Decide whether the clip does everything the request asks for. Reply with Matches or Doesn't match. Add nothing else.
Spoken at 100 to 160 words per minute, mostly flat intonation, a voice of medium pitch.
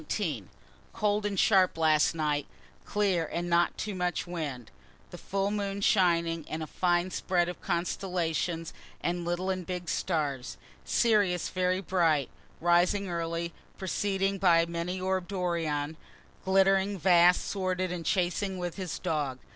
Matches